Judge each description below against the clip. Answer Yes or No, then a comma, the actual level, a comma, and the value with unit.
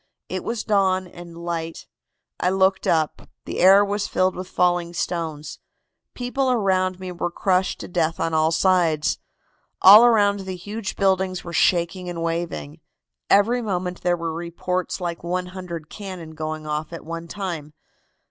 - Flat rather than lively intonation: Yes, narrow, 2.3 semitones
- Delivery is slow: No, average, 155 wpm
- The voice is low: No, medium, 180 Hz